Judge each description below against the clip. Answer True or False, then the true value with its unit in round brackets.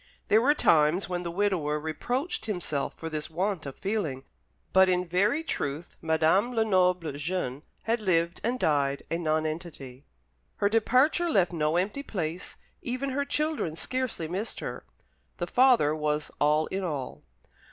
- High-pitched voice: False (180 Hz)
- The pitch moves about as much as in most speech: False (6.2 semitones)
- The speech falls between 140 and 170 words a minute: True (150 wpm)